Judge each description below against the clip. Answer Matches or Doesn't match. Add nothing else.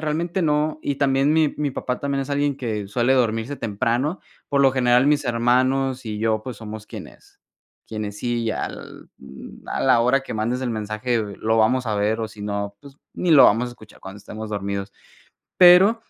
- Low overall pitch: Matches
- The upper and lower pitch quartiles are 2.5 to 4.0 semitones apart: Doesn't match